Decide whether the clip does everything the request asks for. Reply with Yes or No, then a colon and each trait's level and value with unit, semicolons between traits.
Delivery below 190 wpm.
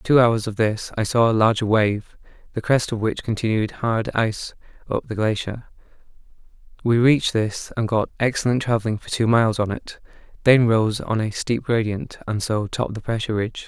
No: average, 195 wpm